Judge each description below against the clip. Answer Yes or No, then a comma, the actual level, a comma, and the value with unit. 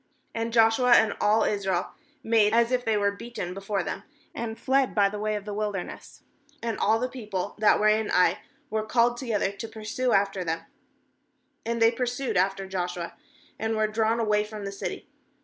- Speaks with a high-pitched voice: Yes, high, 215 Hz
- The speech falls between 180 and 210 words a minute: Yes, average, 190 wpm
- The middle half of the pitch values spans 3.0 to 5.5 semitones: No, narrow, 2.4 semitones